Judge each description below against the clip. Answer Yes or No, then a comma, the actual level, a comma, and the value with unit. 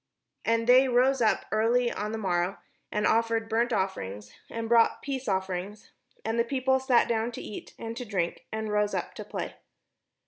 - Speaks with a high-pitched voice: Yes, high, 225 Hz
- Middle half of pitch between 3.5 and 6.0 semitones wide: No, average, 2.7 semitones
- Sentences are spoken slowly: No, average, 180 wpm